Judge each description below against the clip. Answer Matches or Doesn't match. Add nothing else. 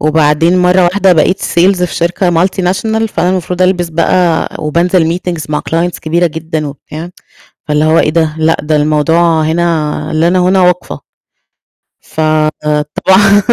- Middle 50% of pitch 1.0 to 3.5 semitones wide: Matches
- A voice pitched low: Doesn't match